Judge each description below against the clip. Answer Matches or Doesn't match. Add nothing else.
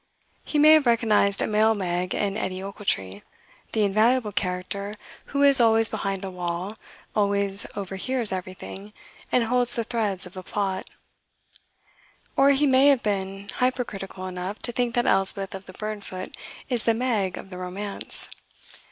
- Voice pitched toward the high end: Matches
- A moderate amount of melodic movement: Matches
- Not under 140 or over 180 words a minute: Matches